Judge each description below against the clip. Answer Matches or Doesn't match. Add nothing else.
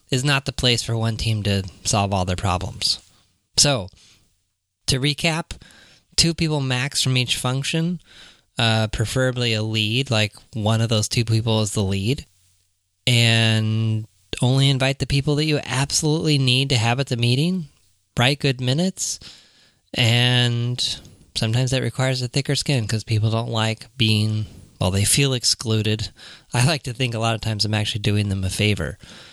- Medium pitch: Doesn't match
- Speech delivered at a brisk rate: Doesn't match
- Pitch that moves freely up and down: Doesn't match